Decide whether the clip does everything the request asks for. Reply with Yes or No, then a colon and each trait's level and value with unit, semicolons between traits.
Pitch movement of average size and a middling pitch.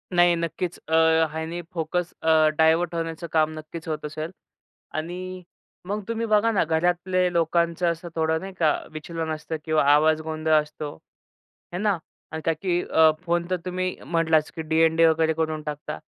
No: narrow, 1.9 semitones; medium, 165 Hz